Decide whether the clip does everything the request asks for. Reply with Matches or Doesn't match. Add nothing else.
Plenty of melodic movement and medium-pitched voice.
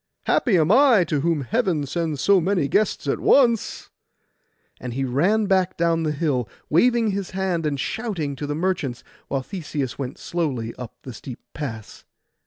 Matches